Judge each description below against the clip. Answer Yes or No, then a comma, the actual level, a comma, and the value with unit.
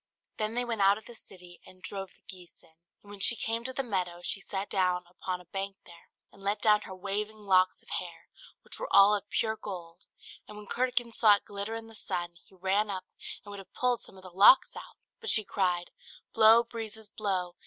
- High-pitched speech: Yes, high, 200 Hz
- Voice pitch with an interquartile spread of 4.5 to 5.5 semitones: No, average, 2.9 semitones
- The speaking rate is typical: No, fast, 230 wpm